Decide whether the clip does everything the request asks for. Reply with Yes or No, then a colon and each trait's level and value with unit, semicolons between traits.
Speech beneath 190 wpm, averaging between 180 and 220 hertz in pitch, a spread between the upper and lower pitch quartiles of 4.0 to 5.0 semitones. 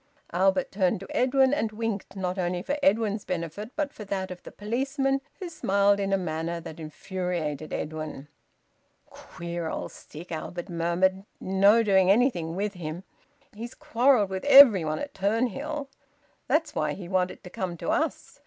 Yes: average, 160 wpm; high, 190 Hz; average, 4.7 semitones